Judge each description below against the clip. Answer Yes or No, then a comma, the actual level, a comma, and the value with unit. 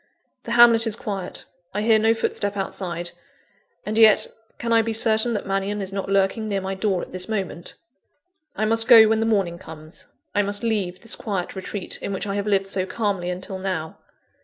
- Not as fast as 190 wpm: No, average, 200 wpm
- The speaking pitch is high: Yes, high, 200 Hz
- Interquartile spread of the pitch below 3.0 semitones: Yes, narrow, 2.6 semitones